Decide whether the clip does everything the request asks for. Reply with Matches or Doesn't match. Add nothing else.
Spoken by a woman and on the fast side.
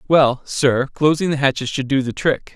Doesn't match